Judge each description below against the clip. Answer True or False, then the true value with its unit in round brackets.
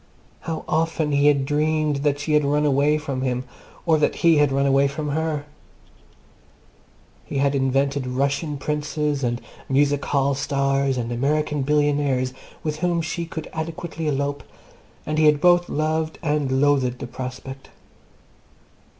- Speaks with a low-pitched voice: False (145 Hz)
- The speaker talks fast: False (150 wpm)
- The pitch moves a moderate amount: False (1.9 semitones)